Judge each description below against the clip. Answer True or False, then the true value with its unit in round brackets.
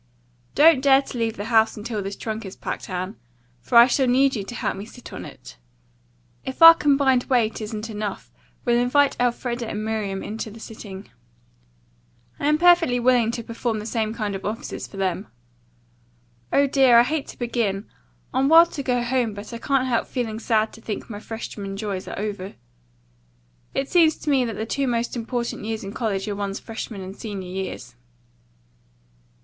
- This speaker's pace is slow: False (190 wpm)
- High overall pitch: True (230 Hz)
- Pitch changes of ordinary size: True (3.5 semitones)